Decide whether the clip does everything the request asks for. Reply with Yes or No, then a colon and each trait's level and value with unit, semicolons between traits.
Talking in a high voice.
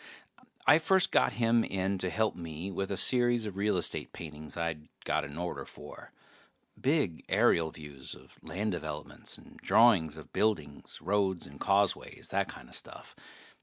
No: very low, 95 Hz